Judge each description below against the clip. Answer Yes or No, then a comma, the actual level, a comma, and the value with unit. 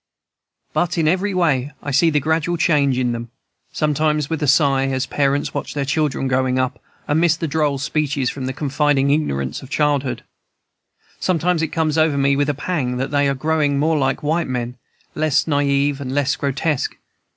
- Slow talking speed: No, average, 185 wpm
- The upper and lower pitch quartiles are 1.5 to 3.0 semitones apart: Yes, narrow, 2.6 semitones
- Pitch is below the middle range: No, medium, 145 Hz